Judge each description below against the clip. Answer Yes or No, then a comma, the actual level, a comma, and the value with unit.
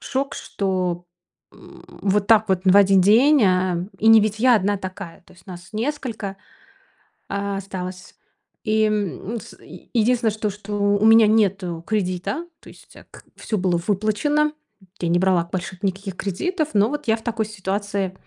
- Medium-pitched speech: No, high, 205 Hz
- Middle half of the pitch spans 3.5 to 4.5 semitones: No, average, 2.8 semitones